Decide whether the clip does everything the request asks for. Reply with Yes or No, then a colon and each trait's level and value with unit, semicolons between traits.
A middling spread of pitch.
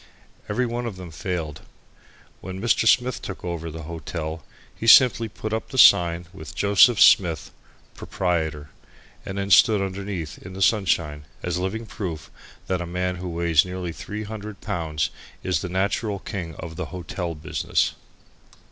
Yes: average, 3.4 semitones